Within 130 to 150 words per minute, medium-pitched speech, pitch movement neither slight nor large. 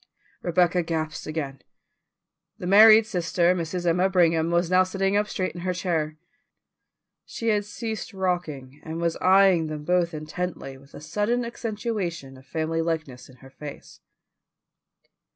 Yes: average, 145 wpm; medium, 175 Hz; average, 3.5 semitones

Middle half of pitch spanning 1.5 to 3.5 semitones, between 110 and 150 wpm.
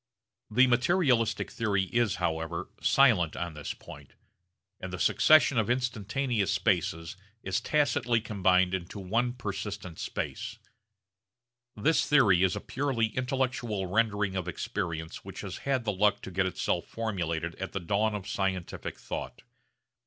No: average, 4.6 semitones; average, 140 wpm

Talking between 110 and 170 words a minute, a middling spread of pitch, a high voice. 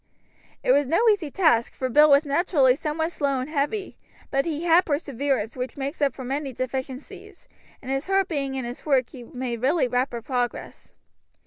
No: average, 185 wpm; average, 3.1 semitones; very high, 275 Hz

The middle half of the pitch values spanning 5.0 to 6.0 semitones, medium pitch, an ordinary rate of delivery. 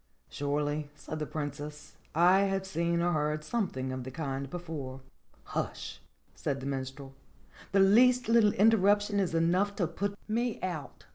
Yes: wide, 5.5 semitones; medium, 165 Hz; average, 160 wpm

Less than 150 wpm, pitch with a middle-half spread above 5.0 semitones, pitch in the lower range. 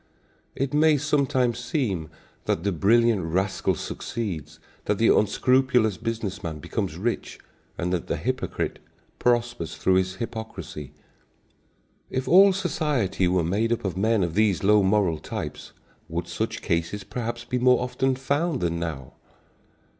Yes: average, 140 wpm; wide, 5.6 semitones; low, 110 Hz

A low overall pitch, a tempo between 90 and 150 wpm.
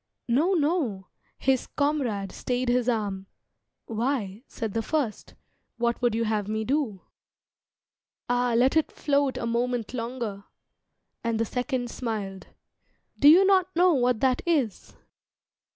No: high, 245 Hz; slow, 135 wpm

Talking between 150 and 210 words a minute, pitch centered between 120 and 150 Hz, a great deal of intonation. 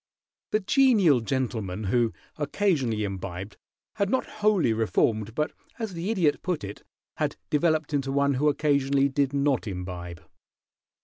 No: slow, 135 wpm; medium, 140 Hz; wide, 7.1 semitones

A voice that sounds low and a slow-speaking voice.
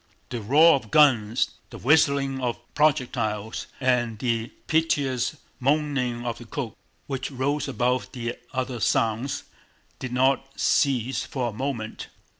Yes: low, 130 Hz; slow, 130 wpm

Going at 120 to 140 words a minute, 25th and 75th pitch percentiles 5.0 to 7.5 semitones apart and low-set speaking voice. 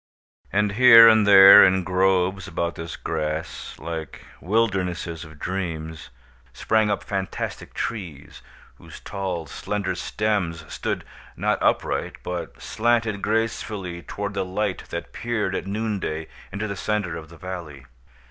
No: slow, 135 wpm; average, 3.8 semitones; very low, 95 Hz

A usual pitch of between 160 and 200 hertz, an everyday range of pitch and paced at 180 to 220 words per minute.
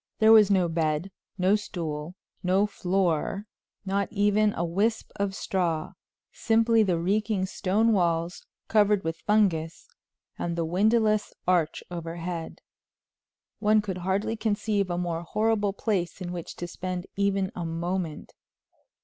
No: high, 190 Hz; average, 3.3 semitones; slow, 135 wpm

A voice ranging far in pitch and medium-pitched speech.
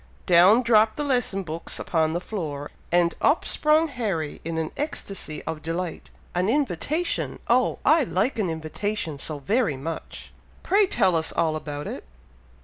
Yes: wide, 7.4 semitones; medium, 180 Hz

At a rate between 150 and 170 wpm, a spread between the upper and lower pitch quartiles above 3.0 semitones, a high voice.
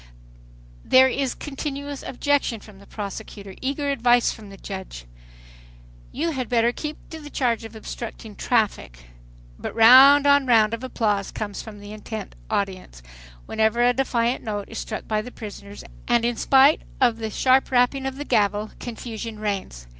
Yes: average, 160 wpm; average, 3.9 semitones; high, 230 Hz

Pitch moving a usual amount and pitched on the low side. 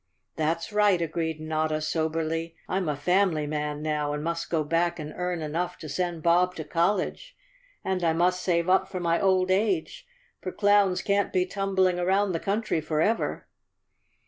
No: average, 3.0 semitones; medium, 170 Hz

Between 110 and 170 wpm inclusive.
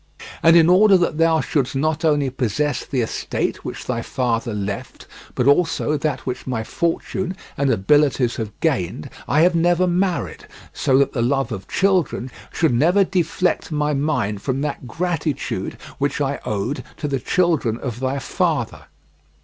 Yes: average, 160 wpm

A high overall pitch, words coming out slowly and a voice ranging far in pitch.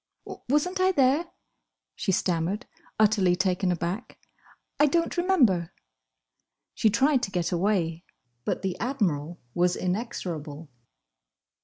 Yes: high, 195 Hz; slow, 110 wpm; wide, 7.1 semitones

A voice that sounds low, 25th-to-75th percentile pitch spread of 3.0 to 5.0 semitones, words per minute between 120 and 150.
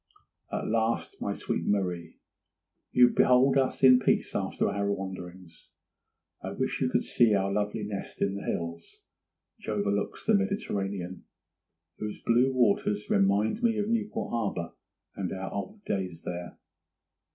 Yes: low, 100 Hz; average, 4.7 semitones; average, 140 wpm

